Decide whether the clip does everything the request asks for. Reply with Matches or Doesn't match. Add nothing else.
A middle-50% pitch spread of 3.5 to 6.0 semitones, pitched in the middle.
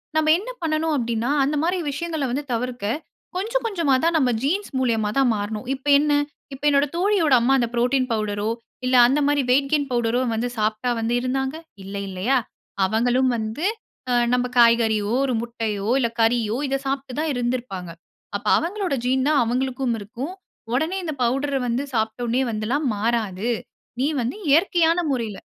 Doesn't match